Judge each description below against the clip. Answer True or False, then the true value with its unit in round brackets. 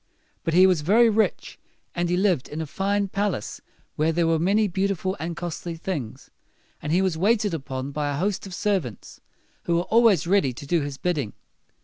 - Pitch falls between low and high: True (175 Hz)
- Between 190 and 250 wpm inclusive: True (195 wpm)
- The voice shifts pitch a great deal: False (4.3 semitones)